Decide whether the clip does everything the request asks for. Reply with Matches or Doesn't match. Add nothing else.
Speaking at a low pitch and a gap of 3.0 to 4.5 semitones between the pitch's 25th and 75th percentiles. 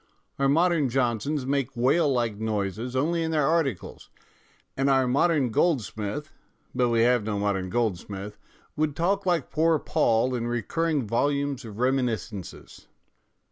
Doesn't match